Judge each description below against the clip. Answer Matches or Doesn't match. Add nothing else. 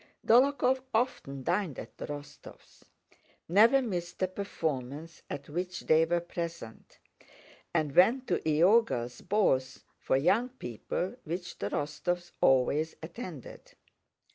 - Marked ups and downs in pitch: Matches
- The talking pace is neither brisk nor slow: Doesn't match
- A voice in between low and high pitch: Matches